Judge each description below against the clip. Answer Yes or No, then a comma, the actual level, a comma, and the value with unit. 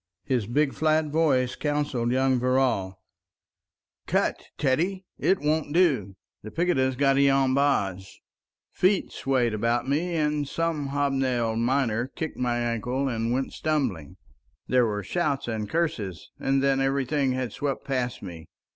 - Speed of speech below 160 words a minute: Yes, average, 140 wpm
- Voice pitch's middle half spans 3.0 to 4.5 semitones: Yes, average, 3.7 semitones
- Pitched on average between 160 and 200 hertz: No, low, 135 Hz